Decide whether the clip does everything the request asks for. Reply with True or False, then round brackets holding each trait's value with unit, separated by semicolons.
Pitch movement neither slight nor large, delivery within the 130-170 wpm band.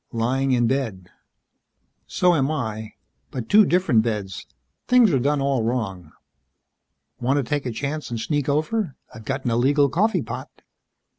True (4.4 semitones; 155 wpm)